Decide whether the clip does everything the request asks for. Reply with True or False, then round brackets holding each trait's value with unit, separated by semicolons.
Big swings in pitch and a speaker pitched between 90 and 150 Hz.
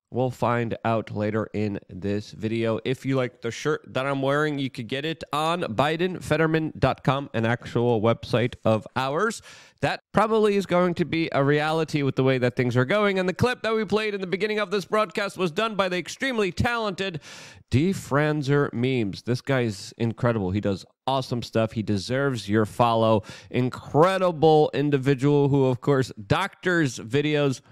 True (5.9 semitones; 135 Hz)